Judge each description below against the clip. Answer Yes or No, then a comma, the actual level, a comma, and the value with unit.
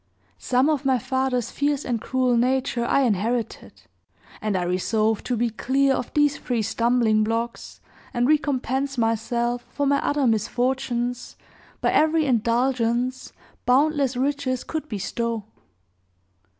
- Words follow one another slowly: Yes, slow, 125 wpm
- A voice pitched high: Yes, very high, 250 Hz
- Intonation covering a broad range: No, narrow, 2.6 semitones